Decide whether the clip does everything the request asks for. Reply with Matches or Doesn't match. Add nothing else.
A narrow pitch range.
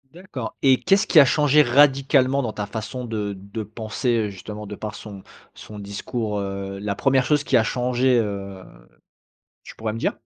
Doesn't match